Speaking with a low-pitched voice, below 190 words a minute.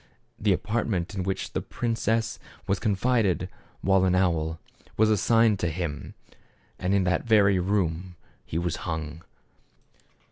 Yes: very low, 95 Hz; average, 140 wpm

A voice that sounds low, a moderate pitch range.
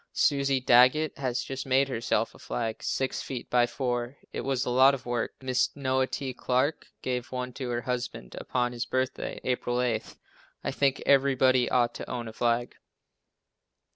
No: low, 125 Hz; narrow, 1.5 semitones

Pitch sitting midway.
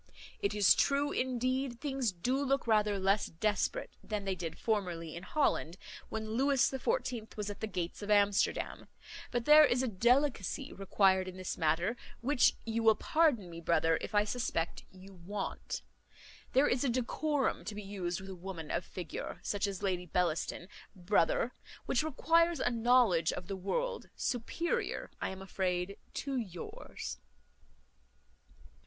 No: high, 210 Hz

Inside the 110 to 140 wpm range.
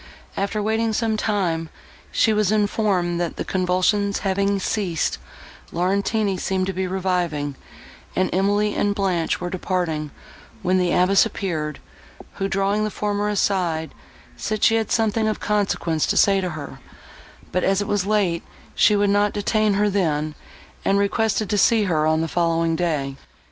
No: average, 160 wpm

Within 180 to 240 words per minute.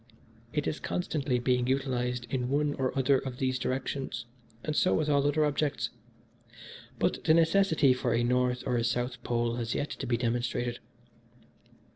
No: average, 165 wpm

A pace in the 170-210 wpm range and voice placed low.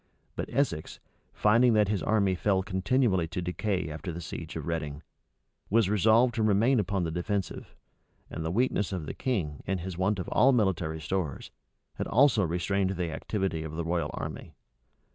Yes: average, 175 wpm; very low, 95 Hz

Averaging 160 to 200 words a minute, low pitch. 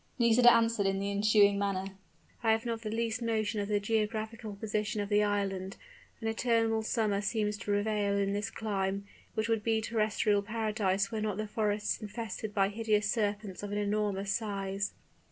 No: average, 180 wpm; high, 210 Hz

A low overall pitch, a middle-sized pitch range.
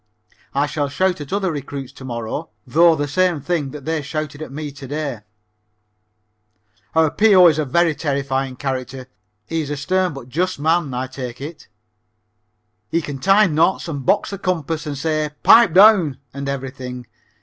No: medium, 150 Hz; average, 3.8 semitones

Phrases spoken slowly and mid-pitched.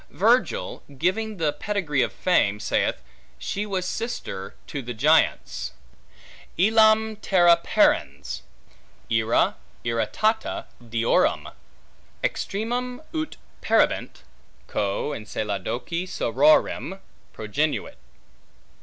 Yes: slow, 85 wpm; medium, 170 Hz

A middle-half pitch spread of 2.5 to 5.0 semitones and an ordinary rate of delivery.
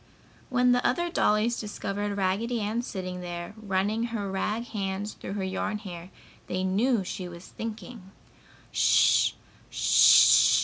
No: average, 3.3 semitones; slow, 125 wpm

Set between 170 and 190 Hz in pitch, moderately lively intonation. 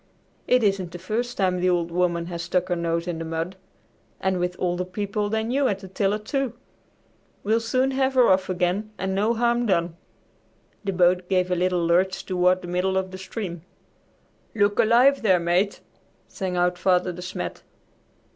Yes: medium, 185 Hz; average, 3.0 semitones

